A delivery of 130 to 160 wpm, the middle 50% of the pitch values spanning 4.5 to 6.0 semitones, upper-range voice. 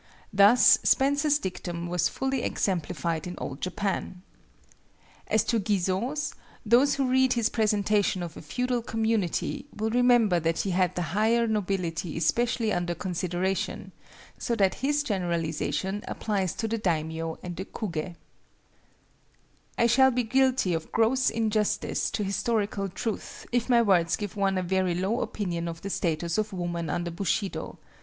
Yes: average, 150 wpm; average, 4.8 semitones; high, 200 Hz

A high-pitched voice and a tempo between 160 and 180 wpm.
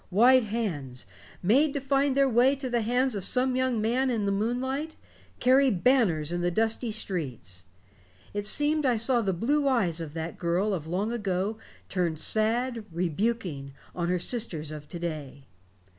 Yes: high, 215 Hz; average, 170 wpm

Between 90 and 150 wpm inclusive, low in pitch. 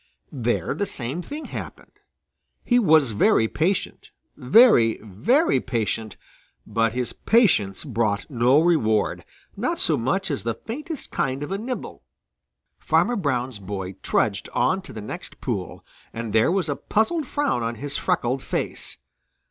Yes: average, 145 wpm; low, 130 Hz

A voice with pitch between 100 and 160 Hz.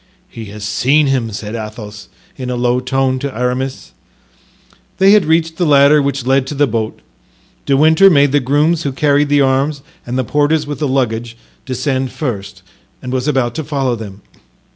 Yes: low, 135 Hz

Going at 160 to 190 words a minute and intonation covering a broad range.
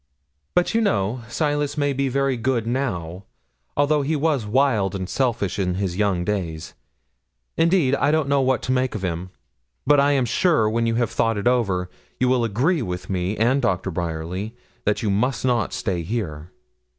Yes: average, 185 wpm; wide, 6.2 semitones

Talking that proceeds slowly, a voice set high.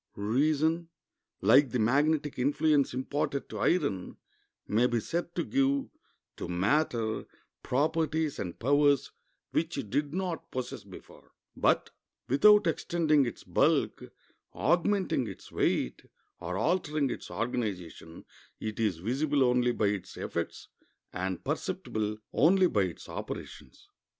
No: slow, 120 wpm; medium, 140 Hz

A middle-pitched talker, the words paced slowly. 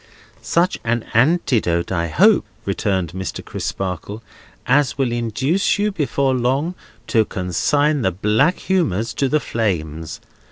No: low, 120 Hz; slow, 125 wpm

